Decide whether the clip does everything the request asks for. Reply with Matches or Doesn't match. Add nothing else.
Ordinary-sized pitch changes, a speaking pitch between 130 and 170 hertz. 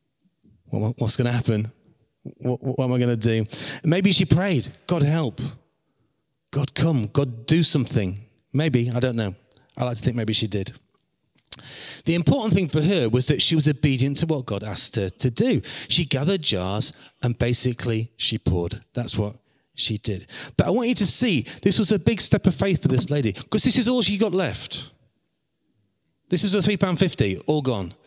Doesn't match